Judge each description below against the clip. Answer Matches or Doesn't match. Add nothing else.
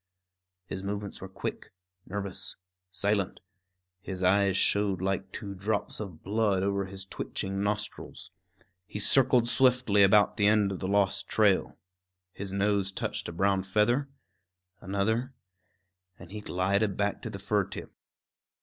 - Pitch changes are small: Matches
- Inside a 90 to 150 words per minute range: Matches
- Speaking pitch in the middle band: Doesn't match